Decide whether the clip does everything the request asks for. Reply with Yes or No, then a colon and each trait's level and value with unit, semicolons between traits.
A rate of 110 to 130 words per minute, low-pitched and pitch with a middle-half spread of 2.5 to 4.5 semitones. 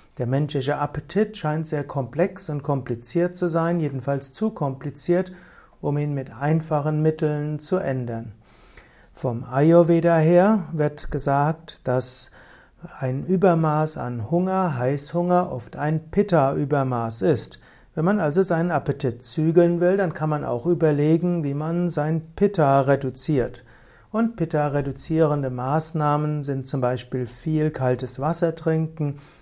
No: slow, 125 wpm; medium, 150 Hz; average, 3.8 semitones